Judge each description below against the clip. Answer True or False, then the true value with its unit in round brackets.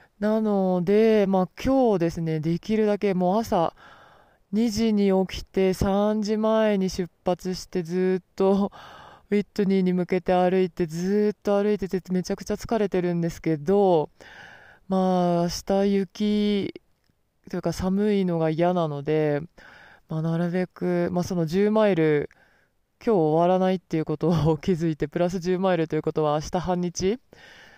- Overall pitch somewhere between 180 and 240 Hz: True (185 Hz)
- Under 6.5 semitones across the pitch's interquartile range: True (2.9 semitones)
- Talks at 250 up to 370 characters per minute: True (285 characters per minute)